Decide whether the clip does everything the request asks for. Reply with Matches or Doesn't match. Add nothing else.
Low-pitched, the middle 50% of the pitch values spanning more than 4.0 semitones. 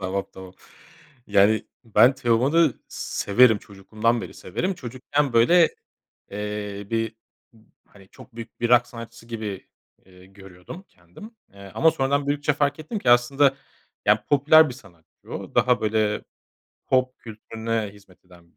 Matches